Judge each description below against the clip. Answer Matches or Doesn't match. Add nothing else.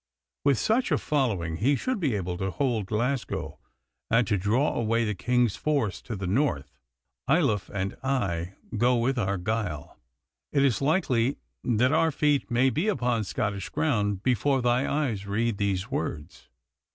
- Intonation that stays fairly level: Doesn't match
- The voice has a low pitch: Matches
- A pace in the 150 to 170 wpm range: Matches